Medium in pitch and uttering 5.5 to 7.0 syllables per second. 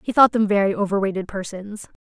No: high, 205 Hz; 6.0 syllables/s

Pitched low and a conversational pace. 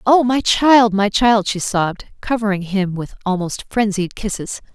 No: high, 210 Hz; average, 165 wpm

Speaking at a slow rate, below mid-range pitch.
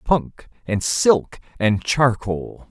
Yes: slow, 110 wpm; low, 120 Hz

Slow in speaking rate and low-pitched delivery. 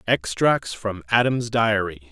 Yes: slow, 115 wpm; low, 105 Hz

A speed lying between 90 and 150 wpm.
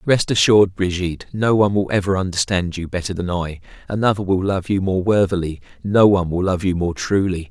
No: average, 200 wpm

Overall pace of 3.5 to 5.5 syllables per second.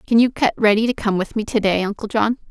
No: 6.2 syllables/s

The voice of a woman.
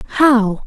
Yes: female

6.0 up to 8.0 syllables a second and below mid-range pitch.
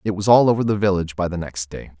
Yes: 7.1 syllables/s; very low, 95 Hz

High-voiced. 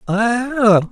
Yes: high, 225 Hz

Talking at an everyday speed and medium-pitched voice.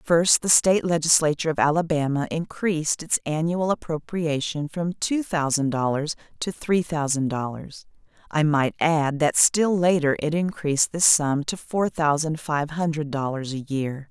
Yes: average, 155 wpm; medium, 155 Hz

